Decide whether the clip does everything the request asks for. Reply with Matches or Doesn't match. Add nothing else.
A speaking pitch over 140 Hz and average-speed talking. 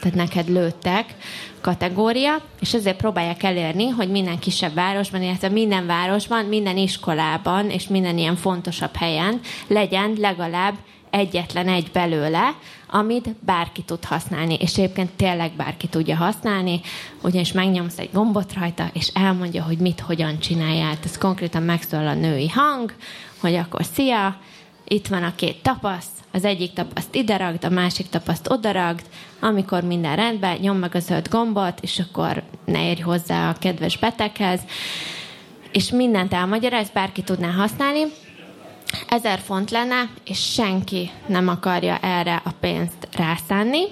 Matches